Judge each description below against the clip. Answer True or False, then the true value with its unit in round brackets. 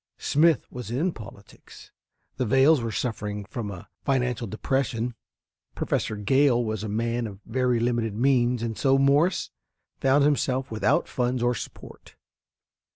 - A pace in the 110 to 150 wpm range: True (140 wpm)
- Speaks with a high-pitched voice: False (120 Hz)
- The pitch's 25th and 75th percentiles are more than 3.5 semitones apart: False (3.1 semitones)